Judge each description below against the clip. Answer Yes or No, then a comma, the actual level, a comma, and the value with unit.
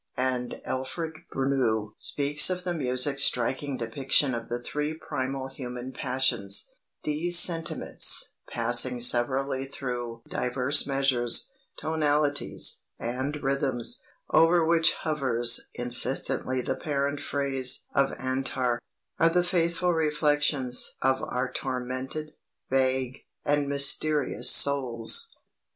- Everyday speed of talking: No, slow, 105 wpm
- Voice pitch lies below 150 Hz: Yes, low, 135 Hz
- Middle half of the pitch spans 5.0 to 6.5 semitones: No, average, 2.8 semitones